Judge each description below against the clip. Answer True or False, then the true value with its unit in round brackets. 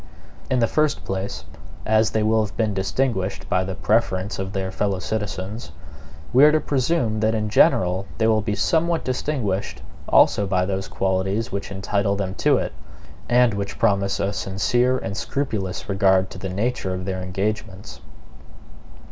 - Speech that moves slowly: False (165 wpm)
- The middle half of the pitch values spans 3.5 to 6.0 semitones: False (2.9 semitones)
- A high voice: False (100 Hz)